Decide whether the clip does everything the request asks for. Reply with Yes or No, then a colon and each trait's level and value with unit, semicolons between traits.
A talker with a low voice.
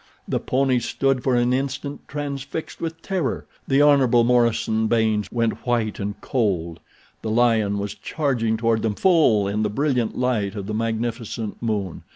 Yes: low, 115 Hz